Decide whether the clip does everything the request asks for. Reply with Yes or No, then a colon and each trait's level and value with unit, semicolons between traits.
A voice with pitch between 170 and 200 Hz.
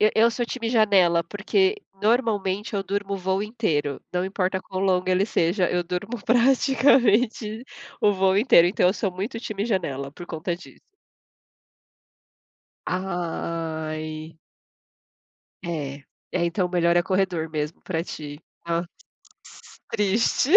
Yes: high, 190 Hz